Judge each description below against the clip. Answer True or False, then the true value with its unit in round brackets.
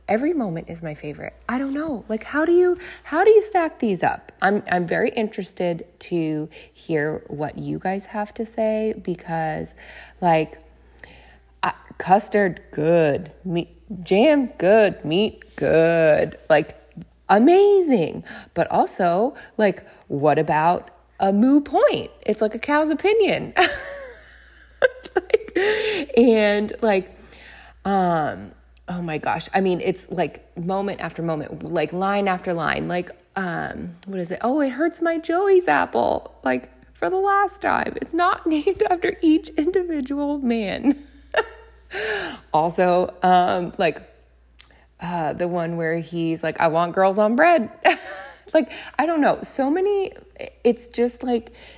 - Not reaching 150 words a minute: True (135 wpm)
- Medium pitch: False (215 Hz)